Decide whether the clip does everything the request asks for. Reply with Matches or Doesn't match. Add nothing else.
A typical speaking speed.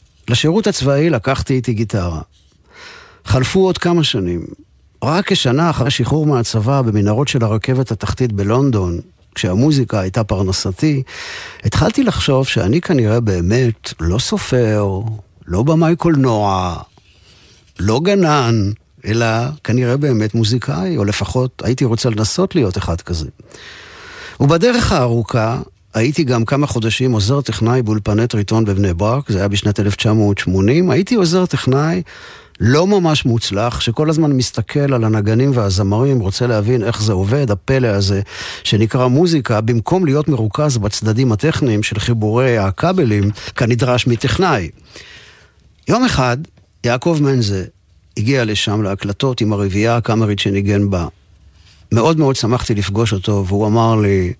Matches